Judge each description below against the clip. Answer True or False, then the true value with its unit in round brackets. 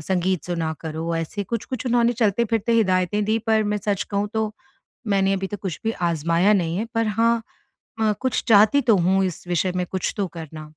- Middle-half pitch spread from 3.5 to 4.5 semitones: True (3.9 semitones)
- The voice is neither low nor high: False (195 Hz)